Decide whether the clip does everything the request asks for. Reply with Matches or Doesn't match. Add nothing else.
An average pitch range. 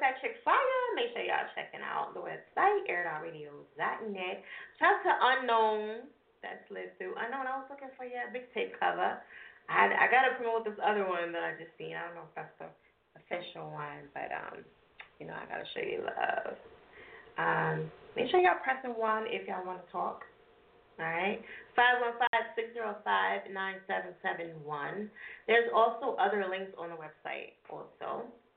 Doesn't match